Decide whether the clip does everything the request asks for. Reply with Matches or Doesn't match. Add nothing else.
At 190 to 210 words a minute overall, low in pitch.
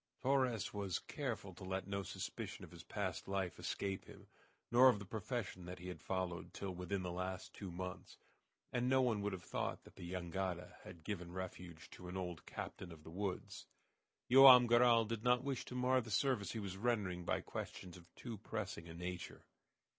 Matches